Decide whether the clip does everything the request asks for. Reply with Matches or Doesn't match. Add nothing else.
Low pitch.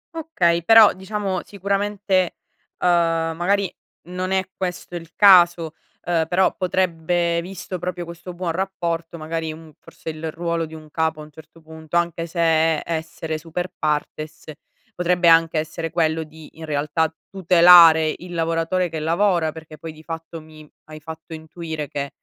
Doesn't match